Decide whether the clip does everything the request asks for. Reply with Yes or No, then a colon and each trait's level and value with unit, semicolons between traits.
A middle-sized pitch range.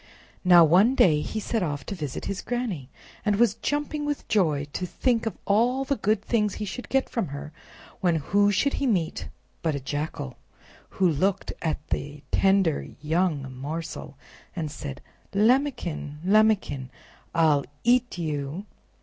No: wide, 6.6 semitones